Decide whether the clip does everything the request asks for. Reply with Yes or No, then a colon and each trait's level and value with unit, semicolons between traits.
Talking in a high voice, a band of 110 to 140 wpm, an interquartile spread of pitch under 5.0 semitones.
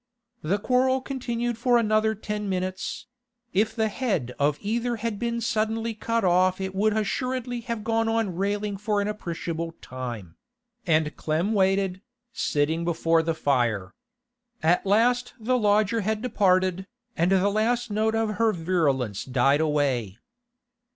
No: high, 205 Hz; slow, 135 wpm; wide, 5.4 semitones